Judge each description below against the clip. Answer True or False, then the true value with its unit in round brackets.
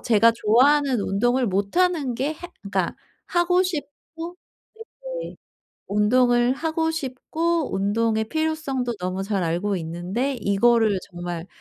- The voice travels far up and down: True (6.9 semitones)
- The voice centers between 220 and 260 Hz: True (240 Hz)